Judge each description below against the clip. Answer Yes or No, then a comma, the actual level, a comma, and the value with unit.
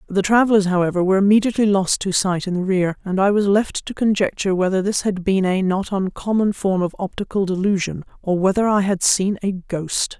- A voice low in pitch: No, high, 195 Hz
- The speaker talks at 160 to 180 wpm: No, fast, 205 wpm